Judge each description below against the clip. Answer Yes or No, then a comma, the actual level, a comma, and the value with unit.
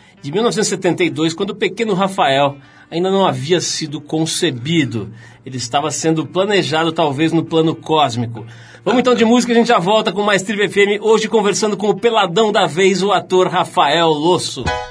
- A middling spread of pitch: Yes, average, 4.6 semitones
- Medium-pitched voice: Yes, medium, 175 Hz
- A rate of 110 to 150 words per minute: No, average, 170 wpm